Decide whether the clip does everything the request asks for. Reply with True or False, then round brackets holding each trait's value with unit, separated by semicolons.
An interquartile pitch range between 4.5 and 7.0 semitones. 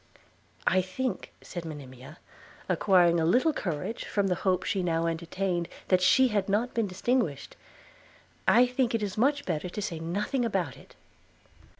True (5.3 semitones)